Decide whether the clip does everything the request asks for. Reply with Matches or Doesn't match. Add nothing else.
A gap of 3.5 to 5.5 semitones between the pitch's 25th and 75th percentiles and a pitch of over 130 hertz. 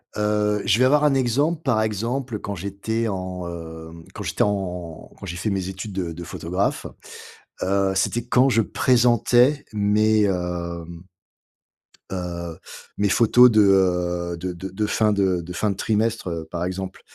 Doesn't match